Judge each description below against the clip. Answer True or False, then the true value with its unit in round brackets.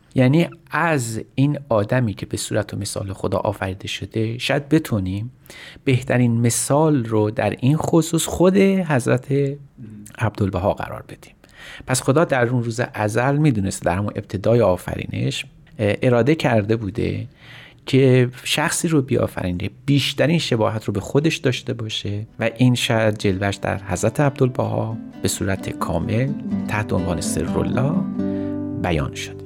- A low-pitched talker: True (120 Hz)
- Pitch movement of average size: True (4.9 semitones)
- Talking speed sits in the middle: True (135 wpm)